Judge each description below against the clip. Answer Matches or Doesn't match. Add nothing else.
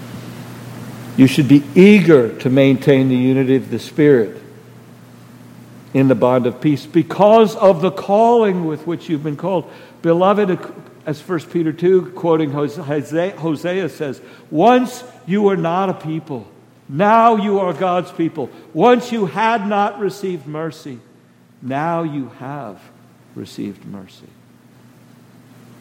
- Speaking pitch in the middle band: Matches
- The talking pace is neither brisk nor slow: Doesn't match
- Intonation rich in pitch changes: Matches